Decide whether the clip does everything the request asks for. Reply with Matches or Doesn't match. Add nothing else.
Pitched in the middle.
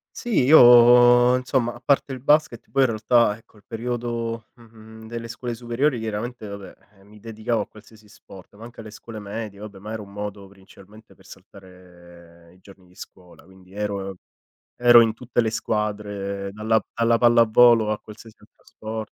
Doesn't match